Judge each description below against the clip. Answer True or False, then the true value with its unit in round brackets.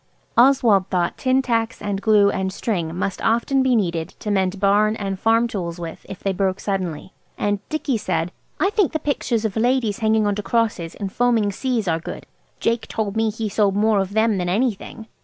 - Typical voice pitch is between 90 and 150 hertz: False (210 Hz)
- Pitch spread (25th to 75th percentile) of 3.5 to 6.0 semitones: False (3.1 semitones)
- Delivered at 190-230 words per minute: True (200 wpm)